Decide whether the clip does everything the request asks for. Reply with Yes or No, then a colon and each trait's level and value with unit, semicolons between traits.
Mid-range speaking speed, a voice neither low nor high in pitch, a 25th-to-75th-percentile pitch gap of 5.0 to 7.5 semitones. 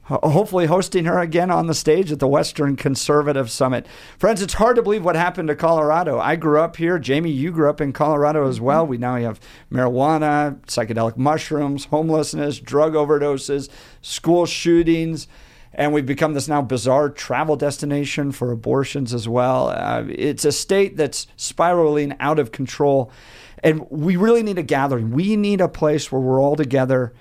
No: average, 175 wpm; medium, 150 Hz; average, 3.3 semitones